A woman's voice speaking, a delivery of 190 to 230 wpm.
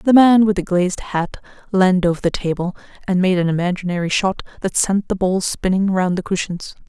Yes: female; average, 200 wpm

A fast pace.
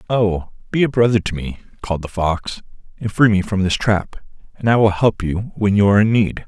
Yes: fast, 230 wpm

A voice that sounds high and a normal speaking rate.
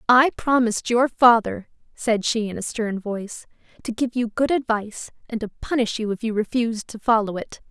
Yes: high, 225 Hz; average, 195 wpm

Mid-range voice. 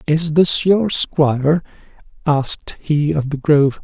Yes: medium, 155 Hz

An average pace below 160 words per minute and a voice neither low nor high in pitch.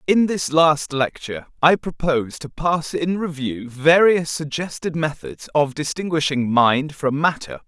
Yes: average, 140 wpm; medium, 150 Hz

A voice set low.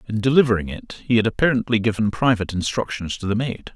Yes: low, 110 Hz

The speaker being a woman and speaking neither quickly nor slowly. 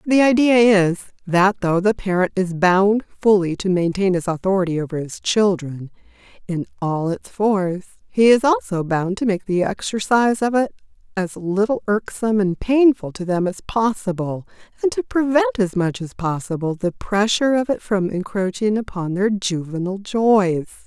Yes: female; average, 165 wpm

